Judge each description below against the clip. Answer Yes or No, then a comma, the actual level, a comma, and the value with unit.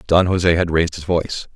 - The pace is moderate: No, fast, 230 wpm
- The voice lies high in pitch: No, very low, 85 Hz